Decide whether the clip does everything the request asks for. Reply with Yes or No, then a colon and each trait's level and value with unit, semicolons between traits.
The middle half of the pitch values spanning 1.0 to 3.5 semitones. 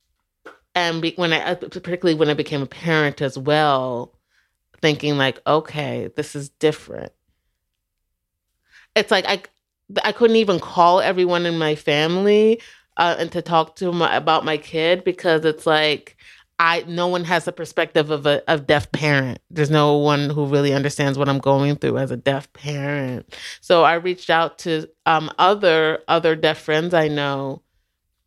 Yes: average, 2.7 semitones